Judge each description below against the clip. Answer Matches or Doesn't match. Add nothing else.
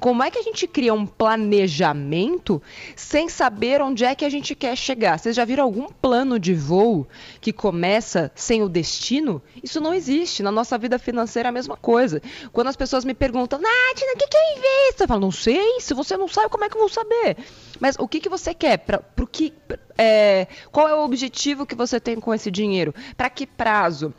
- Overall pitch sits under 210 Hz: Doesn't match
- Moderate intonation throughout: Doesn't match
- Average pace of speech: Doesn't match